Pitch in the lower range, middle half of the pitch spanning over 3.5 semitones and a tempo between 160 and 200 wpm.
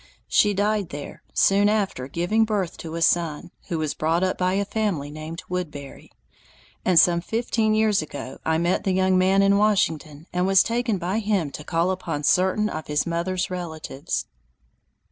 No: medium, 180 Hz; average, 4.0 semitones; average, 175 wpm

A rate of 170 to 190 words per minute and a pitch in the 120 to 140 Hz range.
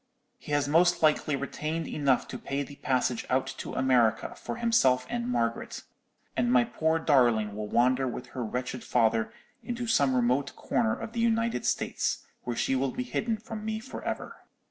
Yes: average, 180 wpm; low, 135 Hz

